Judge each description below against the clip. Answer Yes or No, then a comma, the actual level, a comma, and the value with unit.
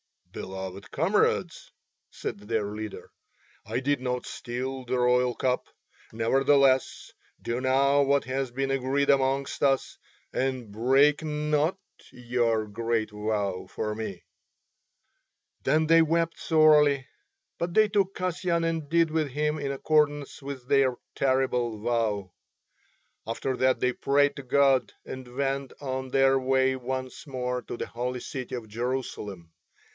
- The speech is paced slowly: Yes, slow, 130 wpm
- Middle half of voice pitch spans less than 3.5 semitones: Yes, average, 2.8 semitones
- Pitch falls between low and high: No, low, 130 Hz